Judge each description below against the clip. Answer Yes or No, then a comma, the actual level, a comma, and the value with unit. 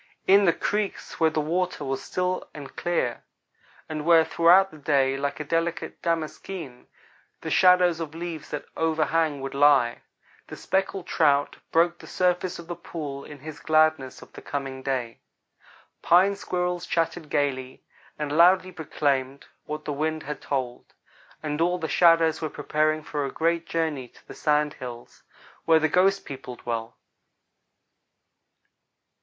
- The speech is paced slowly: No, average, 150 wpm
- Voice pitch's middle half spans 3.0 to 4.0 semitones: Yes, average, 3.4 semitones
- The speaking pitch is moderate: Yes, medium, 155 Hz